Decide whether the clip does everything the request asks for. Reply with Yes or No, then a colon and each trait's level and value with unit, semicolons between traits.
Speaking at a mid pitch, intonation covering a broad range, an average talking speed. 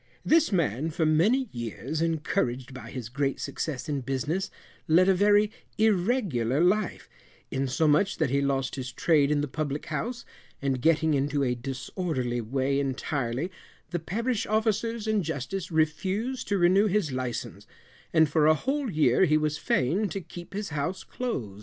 Yes: medium, 155 Hz; wide, 6.3 semitones; average, 160 wpm